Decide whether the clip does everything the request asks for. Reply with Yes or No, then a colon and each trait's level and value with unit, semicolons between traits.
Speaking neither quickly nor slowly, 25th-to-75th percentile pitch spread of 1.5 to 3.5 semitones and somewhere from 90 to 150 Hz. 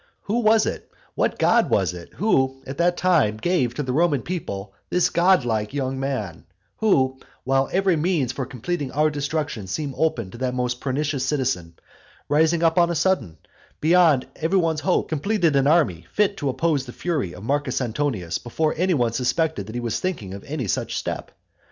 No: average, 190 wpm; wide, 5.5 semitones; medium, 140 Hz